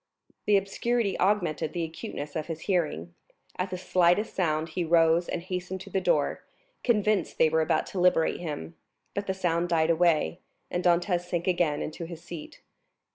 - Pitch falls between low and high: Yes, medium, 175 Hz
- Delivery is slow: No, average, 175 wpm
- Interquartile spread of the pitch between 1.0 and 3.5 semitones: Yes, narrow, 2.5 semitones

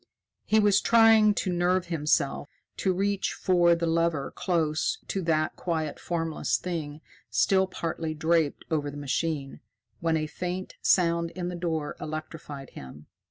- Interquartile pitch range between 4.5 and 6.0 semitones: No, average, 2.7 semitones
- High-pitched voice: No, medium, 165 Hz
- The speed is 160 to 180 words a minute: No, average, 145 wpm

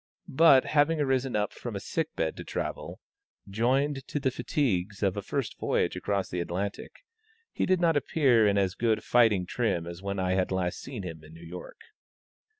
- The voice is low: Yes, low, 105 Hz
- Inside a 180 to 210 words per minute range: Yes, average, 190 wpm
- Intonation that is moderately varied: No, wide, 6.4 semitones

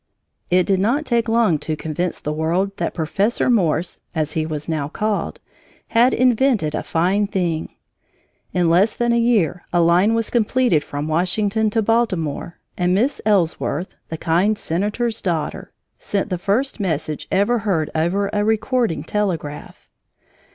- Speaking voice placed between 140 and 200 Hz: Yes, high, 190 Hz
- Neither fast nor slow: Yes, average, 150 wpm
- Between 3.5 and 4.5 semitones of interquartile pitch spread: No, average, 5.2 semitones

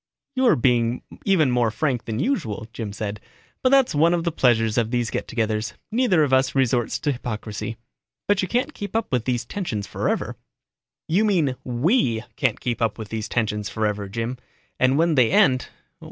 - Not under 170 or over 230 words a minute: Yes, average, 175 wpm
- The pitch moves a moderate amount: No, wide, 6.8 semitones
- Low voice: Yes, low, 125 Hz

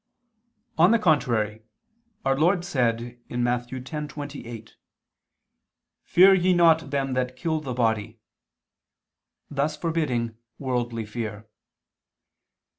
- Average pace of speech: No, slow, 95 wpm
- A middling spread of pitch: Yes, average, 5.0 semitones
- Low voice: Yes, low, 130 Hz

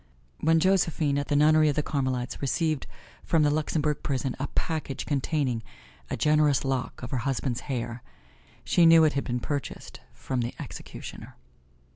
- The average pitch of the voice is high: No, medium, 145 Hz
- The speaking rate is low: No, average, 160 wpm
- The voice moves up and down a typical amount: Yes, average, 3.0 semitones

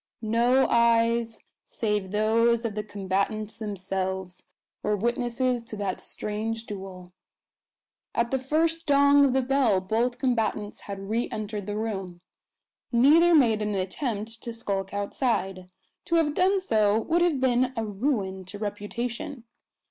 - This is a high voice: Yes, high, 225 Hz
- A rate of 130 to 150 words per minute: Yes, average, 140 wpm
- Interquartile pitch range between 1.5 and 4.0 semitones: Yes, average, 3.7 semitones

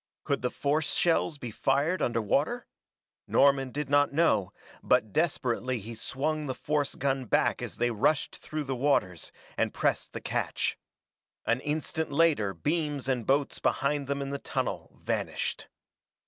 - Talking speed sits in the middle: Yes, average, 155 wpm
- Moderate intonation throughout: Yes, average, 3.0 semitones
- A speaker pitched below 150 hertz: Yes, medium, 140 Hz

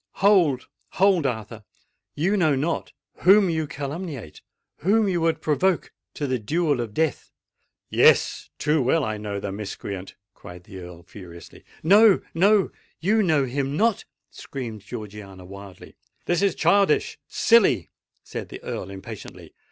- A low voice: No, medium, 145 Hz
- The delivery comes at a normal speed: No, slow, 120 wpm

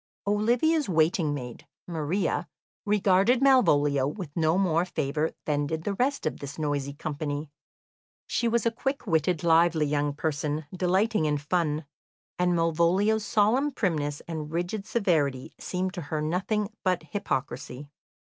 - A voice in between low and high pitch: Yes, medium, 170 Hz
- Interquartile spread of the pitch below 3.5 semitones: No, average, 5.3 semitones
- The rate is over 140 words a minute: No, slow, 135 wpm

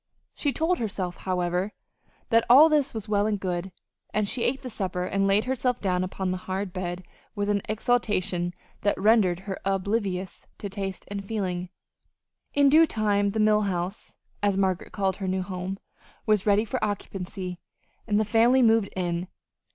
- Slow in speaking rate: No, average, 170 wpm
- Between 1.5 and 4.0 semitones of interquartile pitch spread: Yes, average, 2.8 semitones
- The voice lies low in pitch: No, high, 200 Hz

